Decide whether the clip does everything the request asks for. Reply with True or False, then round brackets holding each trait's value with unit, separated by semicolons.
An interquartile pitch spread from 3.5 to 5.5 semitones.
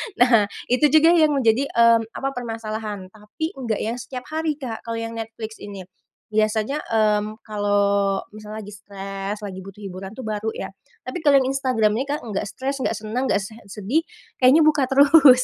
True (4.2 semitones)